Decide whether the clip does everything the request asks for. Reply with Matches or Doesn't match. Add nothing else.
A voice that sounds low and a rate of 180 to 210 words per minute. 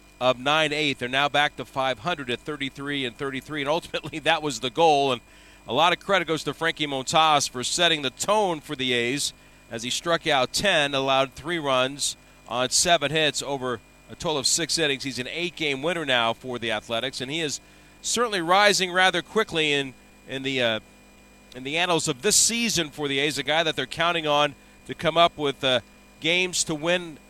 Doesn't match